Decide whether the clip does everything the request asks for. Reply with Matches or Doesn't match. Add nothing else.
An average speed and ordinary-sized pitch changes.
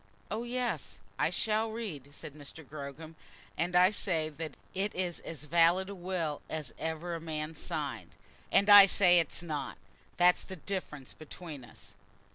Matches